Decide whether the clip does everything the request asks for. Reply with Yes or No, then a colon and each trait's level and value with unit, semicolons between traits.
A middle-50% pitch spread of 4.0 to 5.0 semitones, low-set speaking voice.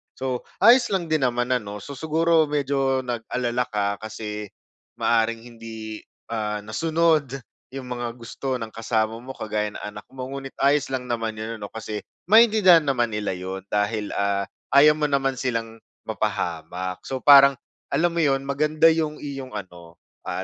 Yes: average, 4.5 semitones; low, 125 Hz